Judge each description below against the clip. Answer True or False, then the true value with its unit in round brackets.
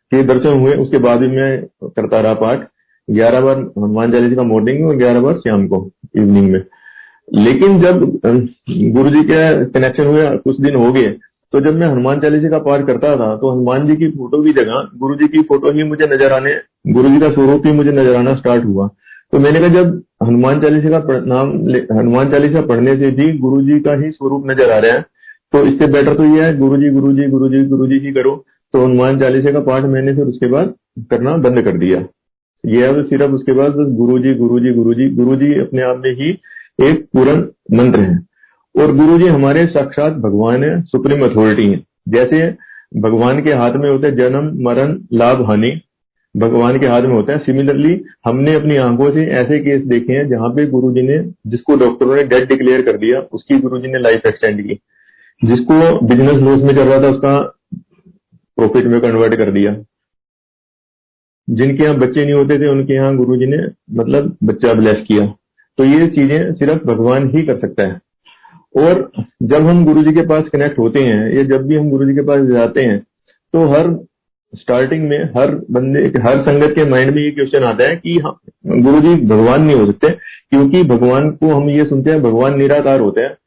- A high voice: False (135 Hz)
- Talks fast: True (200 wpm)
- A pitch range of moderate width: True (3.2 semitones)